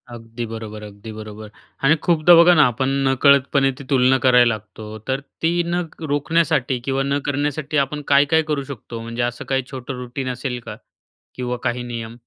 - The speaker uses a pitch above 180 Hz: No, low, 130 Hz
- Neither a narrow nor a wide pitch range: Yes, average, 3.4 semitones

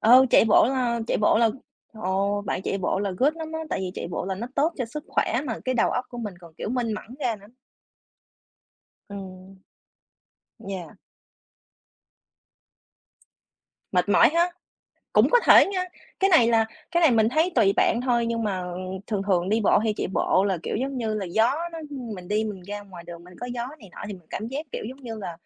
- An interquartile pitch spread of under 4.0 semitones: No, average, 4.6 semitones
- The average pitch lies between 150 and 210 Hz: No, high, 220 Hz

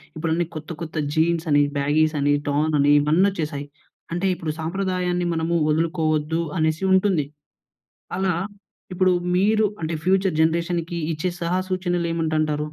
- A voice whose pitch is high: No, medium, 165 Hz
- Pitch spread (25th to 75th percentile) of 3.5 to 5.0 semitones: No, narrow, 2.5 semitones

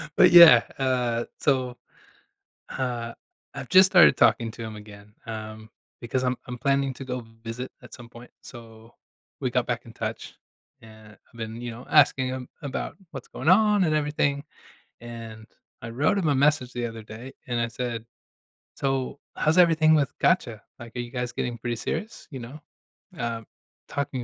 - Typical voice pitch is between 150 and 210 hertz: No, low, 125 Hz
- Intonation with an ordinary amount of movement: Yes, average, 3.3 semitones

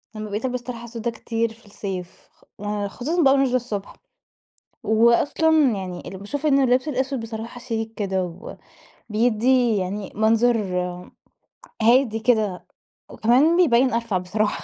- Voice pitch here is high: Yes, high, 230 Hz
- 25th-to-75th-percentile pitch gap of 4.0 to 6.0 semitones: No, average, 3.2 semitones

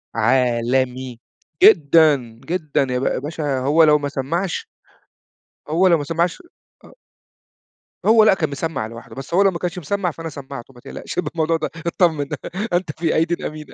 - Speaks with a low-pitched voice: No, medium, 155 Hz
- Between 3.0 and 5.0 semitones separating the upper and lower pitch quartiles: Yes, average, 4.1 semitones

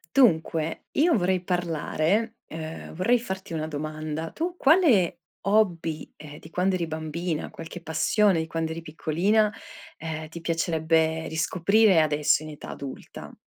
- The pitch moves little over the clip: No, average, 3.2 semitones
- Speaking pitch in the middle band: Yes, medium, 165 Hz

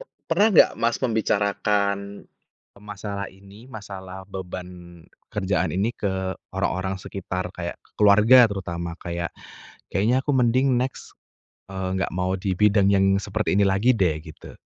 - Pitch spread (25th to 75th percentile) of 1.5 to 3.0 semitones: Yes, narrow, 2.5 semitones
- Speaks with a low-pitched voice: Yes, low, 100 Hz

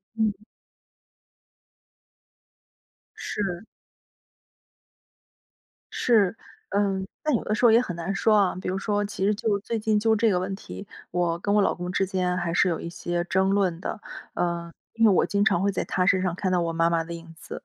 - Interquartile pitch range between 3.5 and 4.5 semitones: No, average, 3.0 semitones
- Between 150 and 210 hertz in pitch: Yes, high, 190 Hz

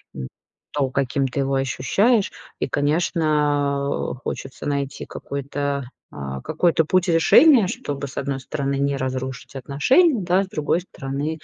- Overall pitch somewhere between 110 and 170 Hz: Yes, medium, 140 Hz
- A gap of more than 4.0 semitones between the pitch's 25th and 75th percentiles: No, average, 3.2 semitones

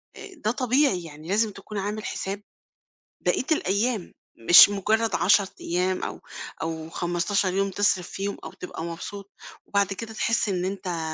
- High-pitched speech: Yes, high, 195 Hz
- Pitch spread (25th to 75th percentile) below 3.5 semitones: Yes, average, 2.9 semitones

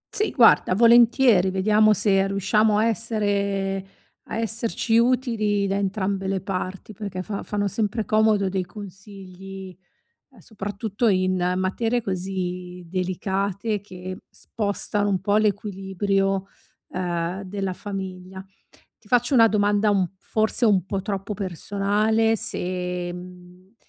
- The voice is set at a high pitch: Yes, high, 195 Hz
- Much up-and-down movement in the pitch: No, narrow, 2.3 semitones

